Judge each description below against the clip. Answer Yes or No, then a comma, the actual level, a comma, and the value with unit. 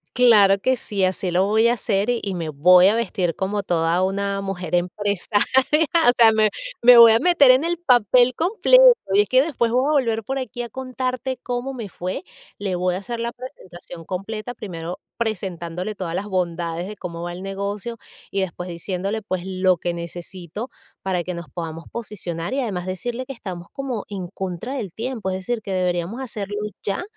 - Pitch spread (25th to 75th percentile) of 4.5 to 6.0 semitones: Yes, average, 5.0 semitones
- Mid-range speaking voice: No, high, 200 Hz